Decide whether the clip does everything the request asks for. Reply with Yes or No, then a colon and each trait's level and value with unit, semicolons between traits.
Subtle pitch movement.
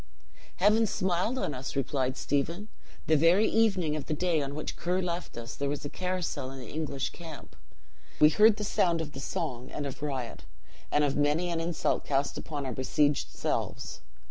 No: average, 4.3 semitones